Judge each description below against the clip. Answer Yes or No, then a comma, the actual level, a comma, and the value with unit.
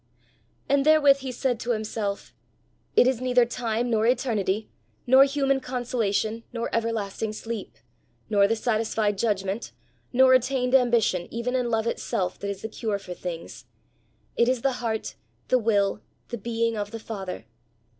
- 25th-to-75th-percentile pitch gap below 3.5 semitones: Yes, average, 2.9 semitones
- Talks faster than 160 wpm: No, average, 155 wpm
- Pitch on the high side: Yes, high, 230 Hz